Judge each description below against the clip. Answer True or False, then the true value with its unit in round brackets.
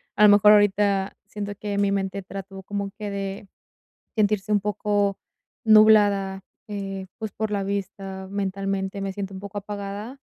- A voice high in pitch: True (200 Hz)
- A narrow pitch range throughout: True (1.0 semitones)